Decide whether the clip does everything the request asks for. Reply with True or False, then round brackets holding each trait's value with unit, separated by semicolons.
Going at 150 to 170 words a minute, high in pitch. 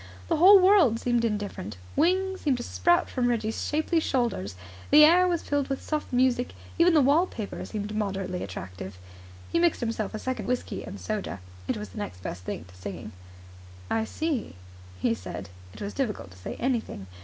False (180 wpm; 240 Hz)